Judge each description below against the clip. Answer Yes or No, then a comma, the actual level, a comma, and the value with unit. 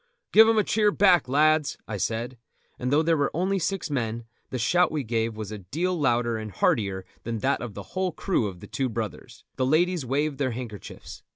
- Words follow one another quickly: Yes, fast, 210 wpm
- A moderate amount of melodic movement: No, wide, 6.9 semitones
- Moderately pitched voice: No, low, 130 Hz